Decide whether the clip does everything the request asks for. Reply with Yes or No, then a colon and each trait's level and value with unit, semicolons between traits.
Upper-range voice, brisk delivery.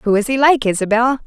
Yes: high, 240 Hz; fast, 240 wpm